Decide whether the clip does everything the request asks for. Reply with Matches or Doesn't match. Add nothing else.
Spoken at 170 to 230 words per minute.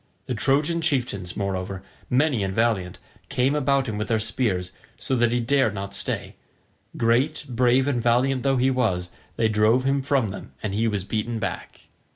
Matches